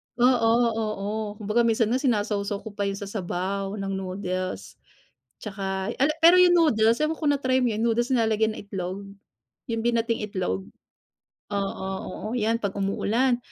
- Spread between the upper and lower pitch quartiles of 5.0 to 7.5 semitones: No, average, 3.2 semitones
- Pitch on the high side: Yes, high, 215 Hz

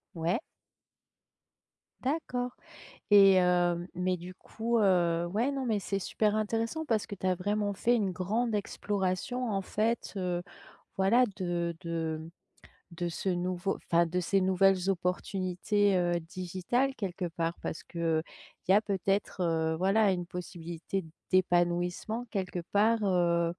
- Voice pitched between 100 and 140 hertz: No, medium, 185 Hz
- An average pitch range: Yes, average, 3.0 semitones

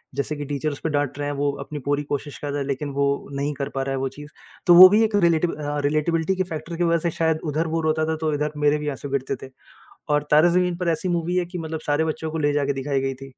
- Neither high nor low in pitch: Yes, medium, 150 Hz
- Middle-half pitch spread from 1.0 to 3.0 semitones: Yes, narrow, 2.6 semitones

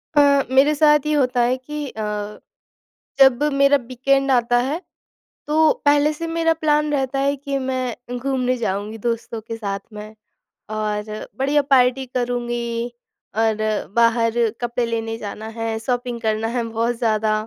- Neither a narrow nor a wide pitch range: Yes, average, 3.5 semitones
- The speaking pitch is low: No, high, 245 Hz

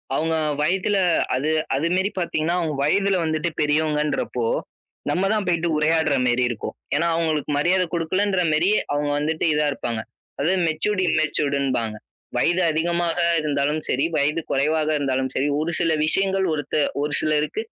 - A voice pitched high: No, medium, 155 Hz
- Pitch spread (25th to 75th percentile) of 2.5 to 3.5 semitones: Yes, average, 2.8 semitones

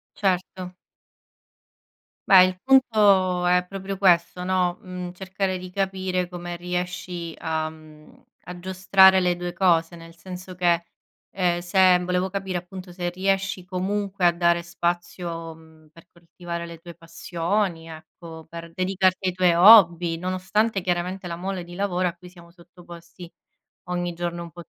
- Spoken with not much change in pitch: Yes, narrow, 1.5 semitones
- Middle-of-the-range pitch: Yes, medium, 180 Hz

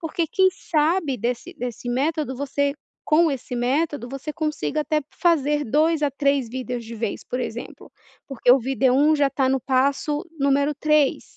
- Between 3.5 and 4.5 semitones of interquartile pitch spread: No, average, 3.1 semitones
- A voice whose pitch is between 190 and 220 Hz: No, very high, 280 Hz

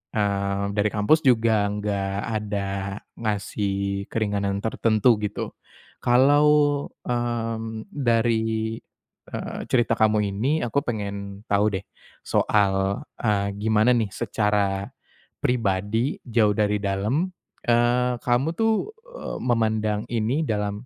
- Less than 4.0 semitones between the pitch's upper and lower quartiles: Yes, average, 2.9 semitones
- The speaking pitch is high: No, low, 110 Hz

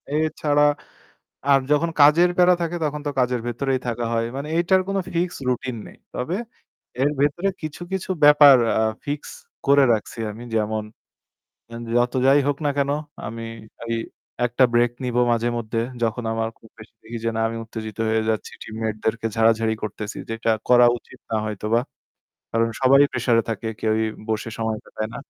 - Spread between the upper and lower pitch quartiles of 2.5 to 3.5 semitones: No, average, 4.3 semitones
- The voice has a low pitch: Yes, low, 120 Hz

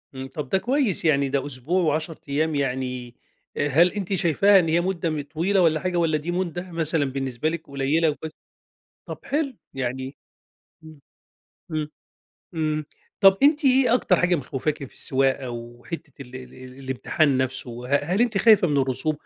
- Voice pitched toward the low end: No, medium, 155 Hz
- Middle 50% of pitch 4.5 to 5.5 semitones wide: Yes, average, 4.8 semitones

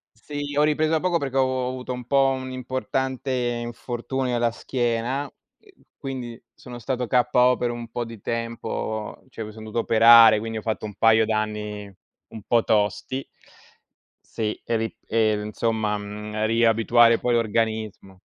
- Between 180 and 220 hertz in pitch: No, low, 115 Hz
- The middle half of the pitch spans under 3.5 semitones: Yes, narrow, 2.6 semitones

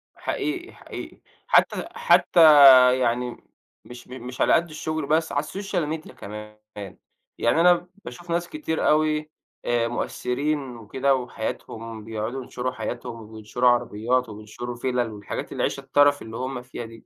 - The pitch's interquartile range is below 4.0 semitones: No, average, 4.9 semitones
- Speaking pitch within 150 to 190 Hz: No, low, 125 Hz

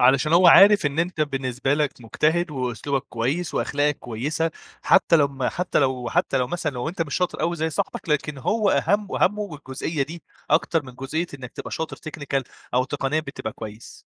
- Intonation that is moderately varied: Yes, average, 4.0 semitones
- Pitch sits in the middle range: Yes, medium, 145 Hz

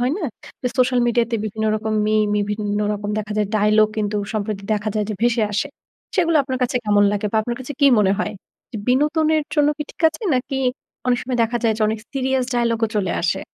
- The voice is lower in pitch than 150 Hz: No, high, 225 Hz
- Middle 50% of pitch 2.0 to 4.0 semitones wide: Yes, average, 3.4 semitones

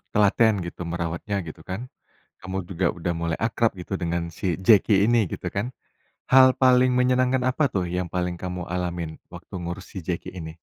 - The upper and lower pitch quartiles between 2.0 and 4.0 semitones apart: No, average, 5.0 semitones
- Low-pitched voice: Yes, very low, 95 Hz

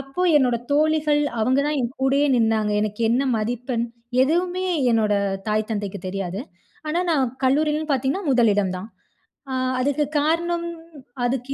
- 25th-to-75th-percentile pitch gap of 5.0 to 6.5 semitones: Yes, wide, 5.6 semitones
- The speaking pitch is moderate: No, very high, 260 Hz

